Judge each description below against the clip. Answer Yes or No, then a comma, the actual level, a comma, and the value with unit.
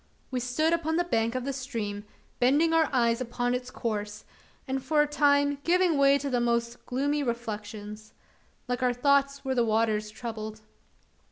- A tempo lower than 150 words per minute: No, average, 170 wpm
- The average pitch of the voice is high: Yes, very high, 250 Hz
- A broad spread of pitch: No, average, 3.8 semitones